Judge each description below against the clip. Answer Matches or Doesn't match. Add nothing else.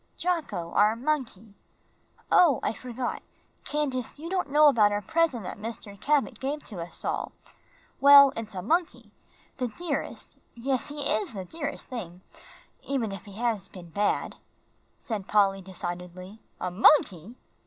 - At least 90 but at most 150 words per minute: Matches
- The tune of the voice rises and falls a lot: Matches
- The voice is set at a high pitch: Matches